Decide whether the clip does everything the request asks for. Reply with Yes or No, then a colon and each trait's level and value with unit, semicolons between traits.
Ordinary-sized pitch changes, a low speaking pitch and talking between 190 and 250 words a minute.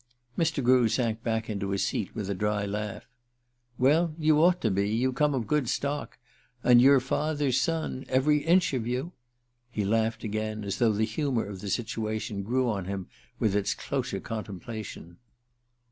No: average, 4.5 semitones; low, 115 Hz; average, 175 wpm